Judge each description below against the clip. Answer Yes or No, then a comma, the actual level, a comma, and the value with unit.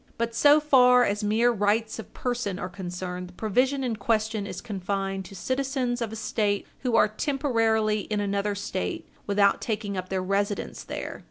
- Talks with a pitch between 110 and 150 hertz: No, high, 215 Hz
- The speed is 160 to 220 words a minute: Yes, average, 175 wpm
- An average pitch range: Yes, average, 3.4 semitones